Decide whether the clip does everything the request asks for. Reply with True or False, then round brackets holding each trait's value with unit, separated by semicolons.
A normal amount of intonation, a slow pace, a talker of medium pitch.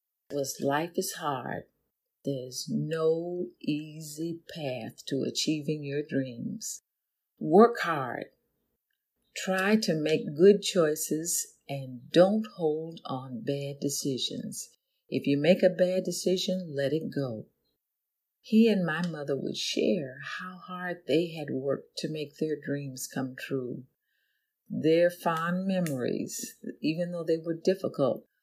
True (4.3 semitones; 125 wpm; 160 Hz)